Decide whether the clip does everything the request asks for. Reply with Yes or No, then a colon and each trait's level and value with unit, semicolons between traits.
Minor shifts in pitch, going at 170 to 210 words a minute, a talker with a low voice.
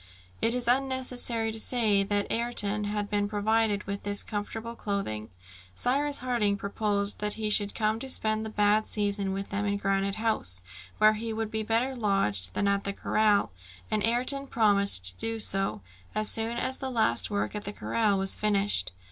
No: narrow, 2.1 semitones; average, 180 wpm; high, 210 Hz